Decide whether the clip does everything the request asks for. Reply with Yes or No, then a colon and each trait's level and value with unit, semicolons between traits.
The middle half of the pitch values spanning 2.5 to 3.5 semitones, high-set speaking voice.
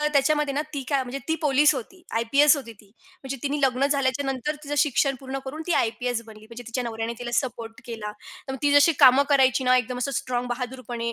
Yes: average, 3.0 semitones; very high, 260 Hz